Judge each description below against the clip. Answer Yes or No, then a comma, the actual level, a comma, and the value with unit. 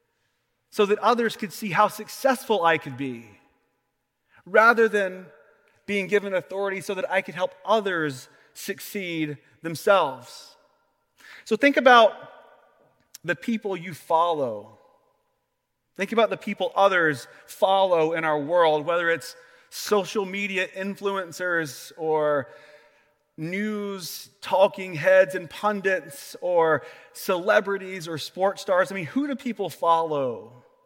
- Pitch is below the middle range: No, high, 195 Hz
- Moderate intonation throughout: Yes, average, 4.3 semitones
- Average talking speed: No, slow, 120 wpm